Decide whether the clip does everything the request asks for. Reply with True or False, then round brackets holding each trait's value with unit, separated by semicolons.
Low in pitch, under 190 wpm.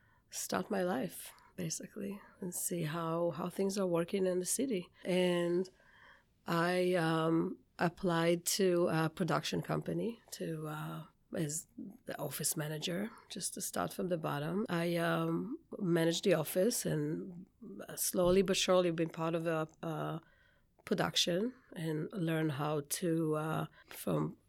False (175 Hz; 135 wpm)